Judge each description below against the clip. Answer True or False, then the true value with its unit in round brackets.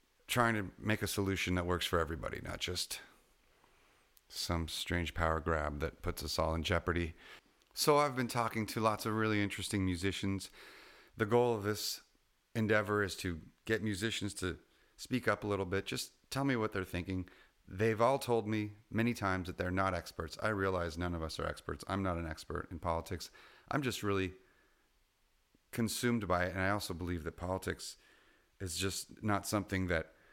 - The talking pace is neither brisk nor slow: True (180 wpm)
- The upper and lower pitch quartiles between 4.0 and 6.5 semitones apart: False (3.5 semitones)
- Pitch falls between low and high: False (95 Hz)